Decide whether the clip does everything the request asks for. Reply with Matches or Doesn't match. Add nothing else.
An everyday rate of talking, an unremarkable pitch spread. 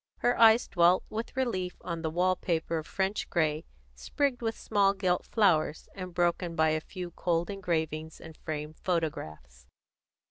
Matches